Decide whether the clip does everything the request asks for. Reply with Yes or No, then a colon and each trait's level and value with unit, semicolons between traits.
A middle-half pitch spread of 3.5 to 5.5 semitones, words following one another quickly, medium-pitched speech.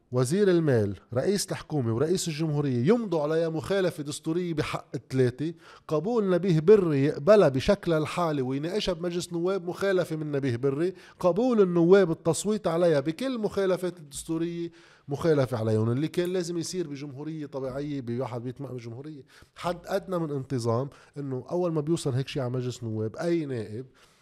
Yes: average, 4.6 semitones; fast, 145 wpm; medium, 160 Hz